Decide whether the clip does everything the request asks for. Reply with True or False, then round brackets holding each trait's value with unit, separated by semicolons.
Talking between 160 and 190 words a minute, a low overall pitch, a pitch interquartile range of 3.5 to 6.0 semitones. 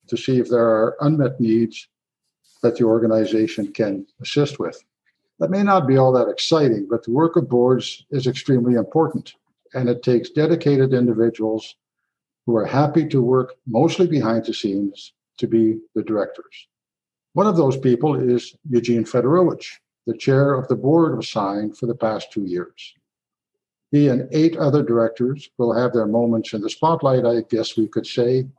True (170 wpm; 125 Hz; 3.8 semitones)